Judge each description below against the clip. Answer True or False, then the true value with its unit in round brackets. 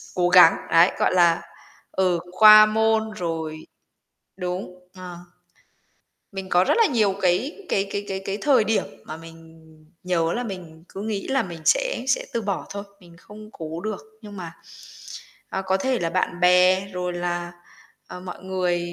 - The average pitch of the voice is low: False (185 Hz)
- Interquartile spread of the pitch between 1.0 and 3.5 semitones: True (3.1 semitones)